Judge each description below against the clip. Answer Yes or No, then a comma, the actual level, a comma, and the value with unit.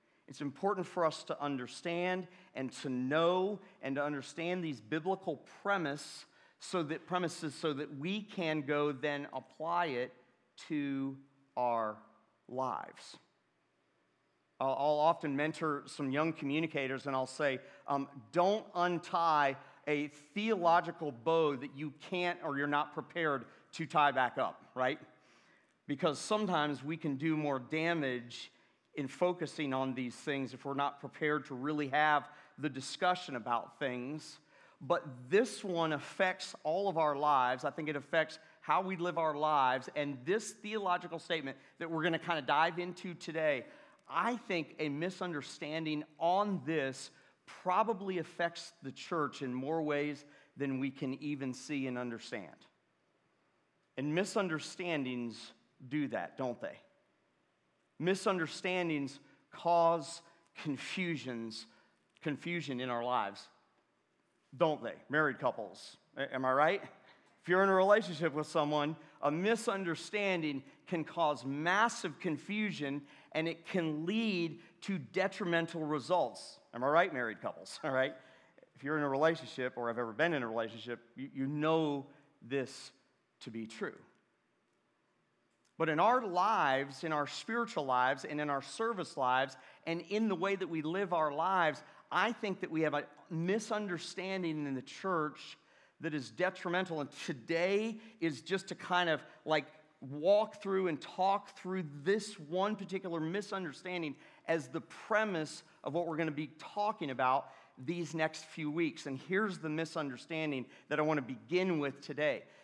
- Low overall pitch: No, medium, 155 Hz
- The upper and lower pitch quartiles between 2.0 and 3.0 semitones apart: No, average, 4.1 semitones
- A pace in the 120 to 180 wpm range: Yes, average, 145 wpm